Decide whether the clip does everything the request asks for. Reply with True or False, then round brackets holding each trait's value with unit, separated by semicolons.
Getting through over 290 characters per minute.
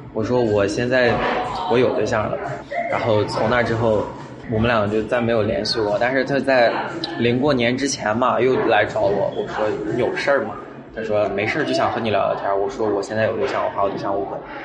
True (305 characters per minute)